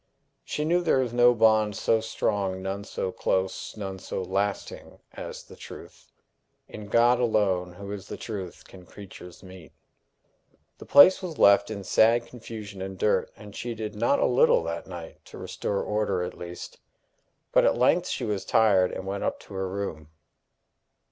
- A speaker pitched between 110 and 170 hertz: No, low, 100 Hz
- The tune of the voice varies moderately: Yes, average, 3.0 semitones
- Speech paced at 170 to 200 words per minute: Yes, average, 175 wpm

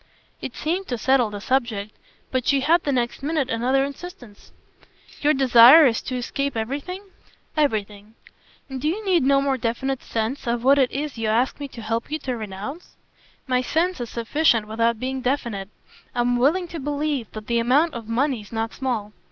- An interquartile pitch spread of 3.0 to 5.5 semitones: Yes, average, 3.7 semitones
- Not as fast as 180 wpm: No, average, 185 wpm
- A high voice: Yes, very high, 255 Hz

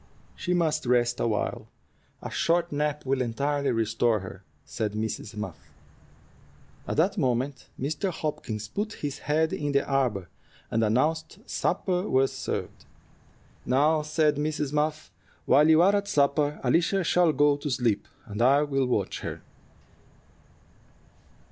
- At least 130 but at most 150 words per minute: Yes, slow, 135 wpm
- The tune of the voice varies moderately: Yes, average, 4.5 semitones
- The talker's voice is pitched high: No, medium, 145 Hz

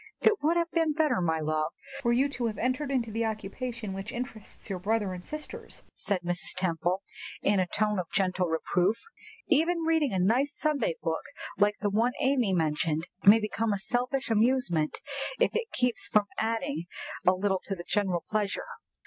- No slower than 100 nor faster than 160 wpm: No, average, 185 wpm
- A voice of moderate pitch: No, high, 215 Hz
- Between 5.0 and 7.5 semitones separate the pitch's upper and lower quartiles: Yes, wide, 5.6 semitones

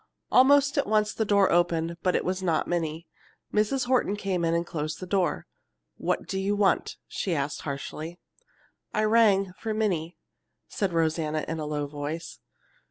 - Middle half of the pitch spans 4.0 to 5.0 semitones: Yes, average, 4.5 semitones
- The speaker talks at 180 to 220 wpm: No, average, 165 wpm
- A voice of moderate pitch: Yes, medium, 180 Hz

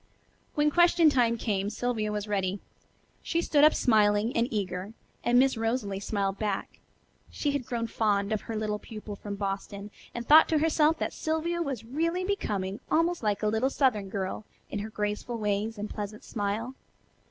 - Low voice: No, high, 220 Hz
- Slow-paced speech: No, average, 175 wpm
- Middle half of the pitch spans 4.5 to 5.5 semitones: Yes, average, 4.8 semitones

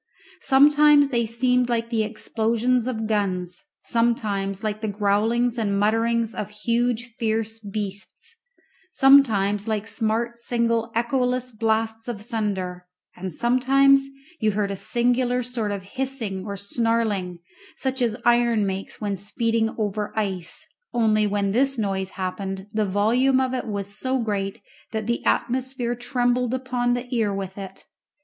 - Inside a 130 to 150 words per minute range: Yes, average, 140 wpm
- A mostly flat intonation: No, average, 3.2 semitones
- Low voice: No, high, 225 Hz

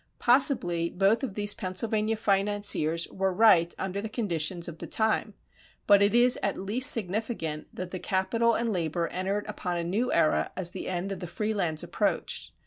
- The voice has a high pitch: Yes, high, 195 Hz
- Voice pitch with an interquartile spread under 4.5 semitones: Yes, average, 3.9 semitones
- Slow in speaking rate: No, average, 175 wpm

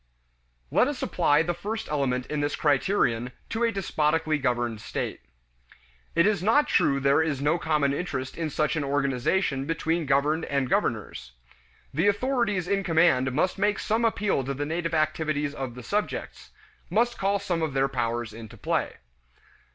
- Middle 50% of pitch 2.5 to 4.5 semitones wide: No, average, 5.2 semitones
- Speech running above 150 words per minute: Yes, average, 165 wpm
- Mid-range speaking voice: Yes, medium, 155 Hz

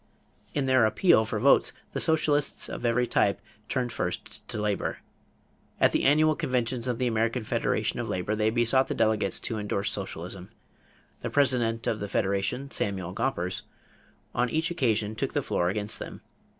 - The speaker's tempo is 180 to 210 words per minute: No, average, 165 wpm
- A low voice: Yes, low, 115 Hz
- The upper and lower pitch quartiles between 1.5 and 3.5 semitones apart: No, average, 4.0 semitones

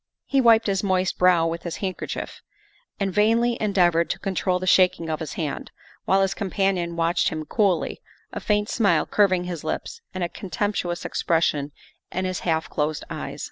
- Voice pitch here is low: No, medium, 185 Hz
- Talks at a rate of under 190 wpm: Yes, average, 175 wpm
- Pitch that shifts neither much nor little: Yes, average, 3.0 semitones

